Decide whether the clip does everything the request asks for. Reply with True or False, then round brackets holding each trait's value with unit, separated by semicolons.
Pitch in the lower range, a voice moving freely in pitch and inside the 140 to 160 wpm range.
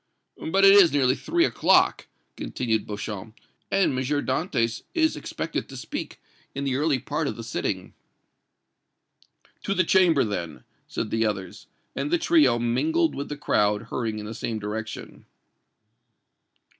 True (130 Hz; 8.0 semitones; 145 wpm)